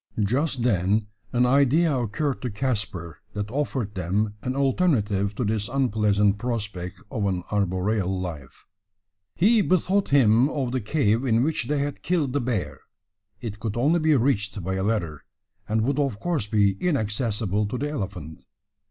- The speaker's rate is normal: Yes, average, 160 wpm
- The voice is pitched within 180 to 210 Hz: No, low, 110 Hz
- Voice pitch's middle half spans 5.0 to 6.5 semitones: Yes, average, 5.3 semitones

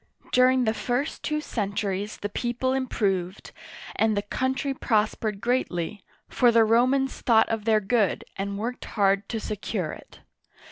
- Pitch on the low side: No, high, 220 Hz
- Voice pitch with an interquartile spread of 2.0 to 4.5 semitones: Yes, average, 3.6 semitones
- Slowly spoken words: No, average, 150 wpm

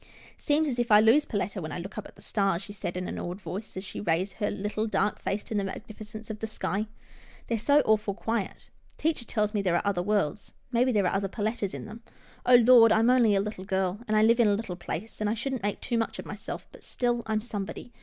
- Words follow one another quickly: Yes, fast, 265 wpm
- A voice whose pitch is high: Yes, high, 210 Hz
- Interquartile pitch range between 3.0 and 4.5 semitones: No, narrow, 2.6 semitones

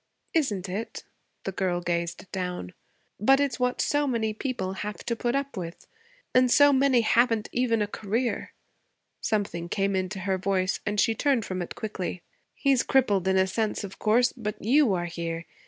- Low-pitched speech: No, high, 210 Hz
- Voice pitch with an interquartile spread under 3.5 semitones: No, average, 4.8 semitones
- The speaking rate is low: No, average, 175 wpm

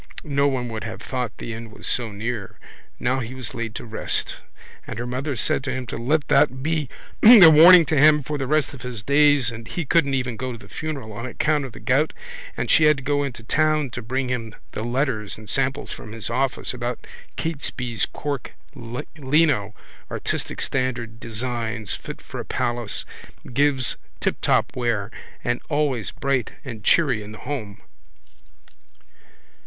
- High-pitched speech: No, low, 130 Hz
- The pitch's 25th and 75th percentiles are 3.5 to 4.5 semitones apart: Yes, average, 3.9 semitones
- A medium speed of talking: Yes, average, 180 wpm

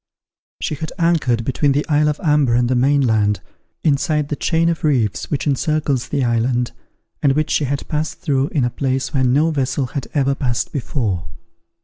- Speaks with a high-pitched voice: No, medium, 140 Hz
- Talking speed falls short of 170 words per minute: No, average, 190 wpm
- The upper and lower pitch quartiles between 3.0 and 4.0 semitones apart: Yes, average, 3.3 semitones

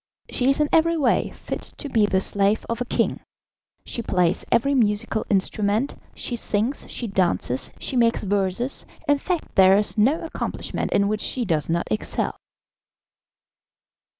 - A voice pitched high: Yes, high, 215 Hz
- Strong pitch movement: No, average, 4.8 semitones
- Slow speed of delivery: No, average, 155 wpm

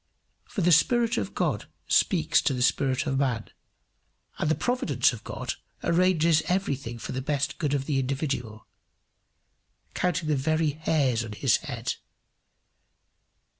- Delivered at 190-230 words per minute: No, average, 145 wpm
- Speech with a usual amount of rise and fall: Yes, average, 4.0 semitones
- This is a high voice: No, medium, 150 Hz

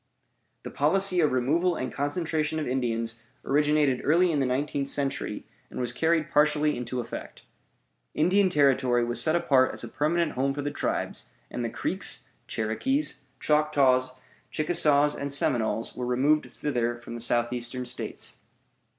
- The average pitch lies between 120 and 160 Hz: Yes, medium, 140 Hz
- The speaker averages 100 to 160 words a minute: Yes, average, 150 wpm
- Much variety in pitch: No, average, 3.5 semitones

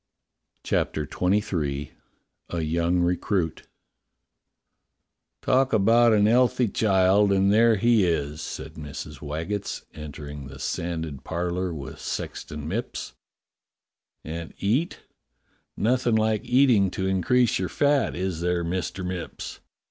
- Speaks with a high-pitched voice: No, very low, 95 Hz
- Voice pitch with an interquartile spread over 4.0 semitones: Yes, average, 5.3 semitones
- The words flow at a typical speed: No, slow, 115 wpm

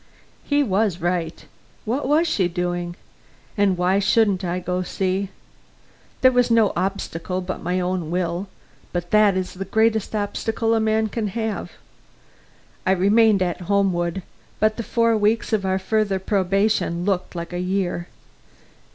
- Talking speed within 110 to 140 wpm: No, average, 150 wpm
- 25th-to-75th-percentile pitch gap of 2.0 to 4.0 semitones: Yes, average, 3.3 semitones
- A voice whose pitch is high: Yes, high, 195 Hz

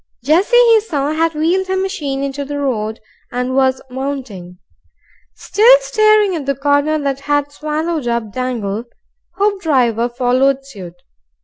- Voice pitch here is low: No, very high, 280 Hz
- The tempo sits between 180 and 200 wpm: No, slow, 135 wpm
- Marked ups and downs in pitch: No, average, 4.7 semitones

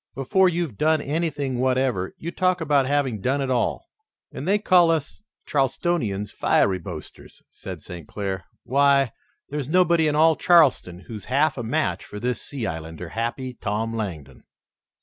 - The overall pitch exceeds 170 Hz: No, low, 135 Hz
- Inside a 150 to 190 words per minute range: Yes, average, 155 wpm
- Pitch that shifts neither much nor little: No, wide, 6.2 semitones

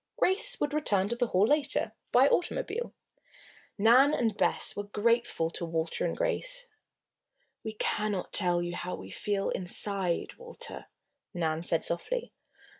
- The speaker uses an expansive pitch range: Yes, wide, 8.6 semitones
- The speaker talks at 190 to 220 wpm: No, average, 140 wpm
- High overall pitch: Yes, high, 210 Hz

